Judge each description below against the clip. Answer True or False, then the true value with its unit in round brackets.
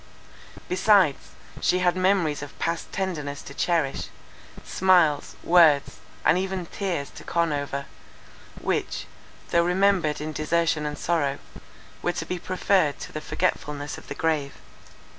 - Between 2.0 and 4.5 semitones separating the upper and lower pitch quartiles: True (3.7 semitones)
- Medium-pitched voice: True (165 Hz)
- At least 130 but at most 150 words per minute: True (135 wpm)